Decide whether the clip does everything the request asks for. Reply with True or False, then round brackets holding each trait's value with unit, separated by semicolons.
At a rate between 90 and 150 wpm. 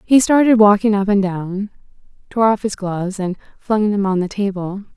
False (180 wpm)